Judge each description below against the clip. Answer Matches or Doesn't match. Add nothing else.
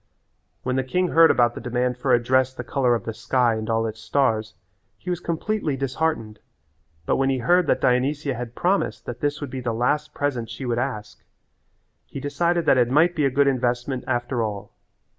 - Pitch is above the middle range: Doesn't match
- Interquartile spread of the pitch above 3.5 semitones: Doesn't match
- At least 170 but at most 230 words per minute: Matches